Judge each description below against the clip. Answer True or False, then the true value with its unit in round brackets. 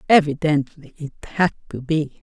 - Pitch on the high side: False (150 Hz)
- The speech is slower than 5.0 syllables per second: True (4.6 syllables/s)